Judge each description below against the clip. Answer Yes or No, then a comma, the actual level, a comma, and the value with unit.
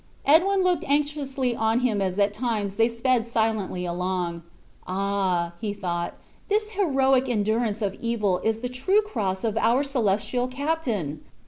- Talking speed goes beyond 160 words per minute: No, average, 145 wpm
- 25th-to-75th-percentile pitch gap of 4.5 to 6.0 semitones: Yes, average, 5.2 semitones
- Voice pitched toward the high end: Yes, high, 225 Hz